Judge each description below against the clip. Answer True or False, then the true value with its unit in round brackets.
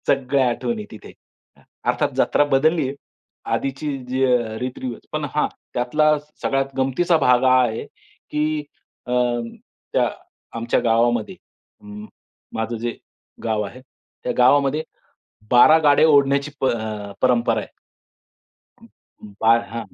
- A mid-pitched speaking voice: False (130 Hz)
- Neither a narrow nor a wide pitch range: True (3.1 semitones)